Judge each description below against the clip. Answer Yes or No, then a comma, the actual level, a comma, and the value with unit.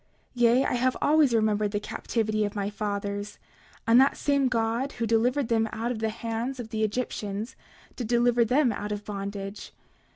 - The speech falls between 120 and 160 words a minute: No, average, 185 wpm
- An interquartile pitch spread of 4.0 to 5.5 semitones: No, average, 2.8 semitones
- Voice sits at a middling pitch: No, high, 225 Hz